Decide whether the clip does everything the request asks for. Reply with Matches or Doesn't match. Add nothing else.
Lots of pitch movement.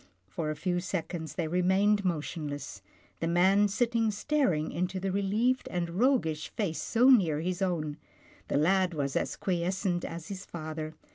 Doesn't match